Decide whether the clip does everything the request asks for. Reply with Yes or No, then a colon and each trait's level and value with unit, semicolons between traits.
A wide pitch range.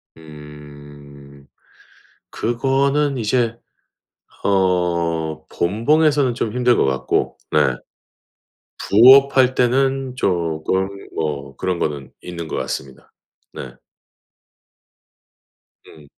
Yes: wide, 9.0 semitones